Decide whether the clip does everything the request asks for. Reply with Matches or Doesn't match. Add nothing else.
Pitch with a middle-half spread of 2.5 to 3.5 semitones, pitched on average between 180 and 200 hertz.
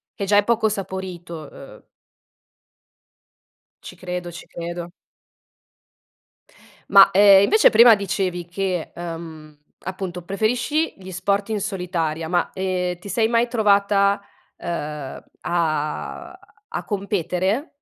Matches